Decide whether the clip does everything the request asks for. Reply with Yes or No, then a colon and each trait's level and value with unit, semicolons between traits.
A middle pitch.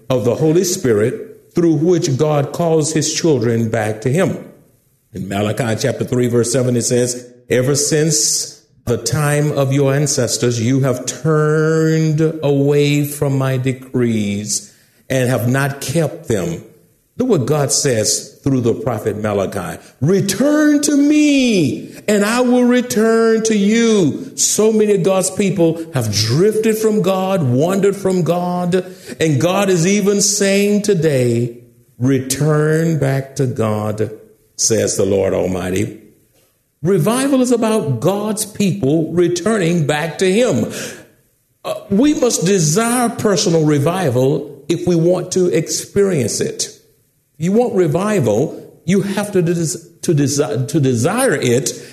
Yes: medium, 155 Hz